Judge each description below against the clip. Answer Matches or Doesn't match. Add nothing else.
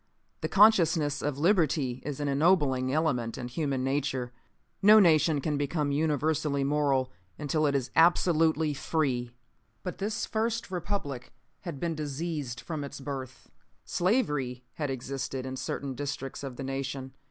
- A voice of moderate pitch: Matches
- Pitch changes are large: Doesn't match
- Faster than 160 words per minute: Doesn't match